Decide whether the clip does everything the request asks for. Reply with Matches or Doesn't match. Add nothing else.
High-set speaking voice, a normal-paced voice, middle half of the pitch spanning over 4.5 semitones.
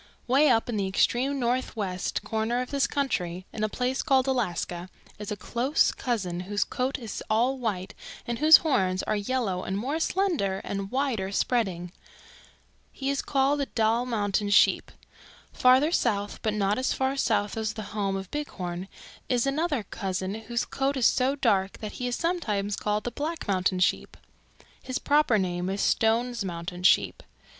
Matches